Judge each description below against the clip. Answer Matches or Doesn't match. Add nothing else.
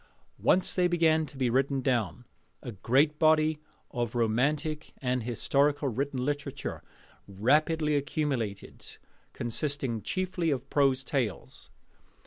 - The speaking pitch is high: Doesn't match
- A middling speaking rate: Doesn't match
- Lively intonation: Doesn't match